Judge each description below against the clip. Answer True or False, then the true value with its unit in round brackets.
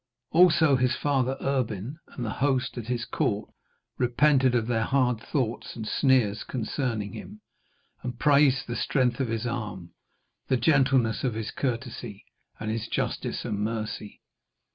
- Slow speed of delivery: False (145 wpm)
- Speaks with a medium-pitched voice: False (125 Hz)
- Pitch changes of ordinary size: True (3.3 semitones)